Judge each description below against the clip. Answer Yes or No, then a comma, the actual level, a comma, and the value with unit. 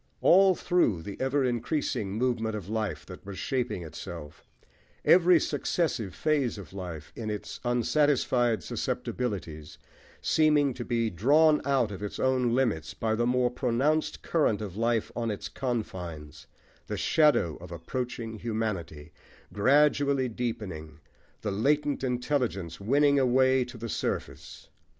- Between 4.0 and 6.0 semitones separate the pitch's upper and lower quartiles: Yes, average, 5.2 semitones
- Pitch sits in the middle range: No, low, 120 Hz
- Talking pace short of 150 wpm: Yes, slow, 135 wpm